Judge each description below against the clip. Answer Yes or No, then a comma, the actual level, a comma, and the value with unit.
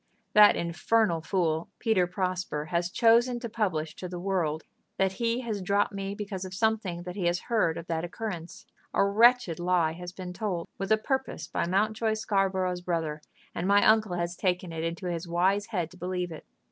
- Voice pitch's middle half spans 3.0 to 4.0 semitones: Yes, average, 3.5 semitones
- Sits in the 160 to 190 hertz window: Yes, medium, 185 Hz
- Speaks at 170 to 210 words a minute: Yes, average, 190 wpm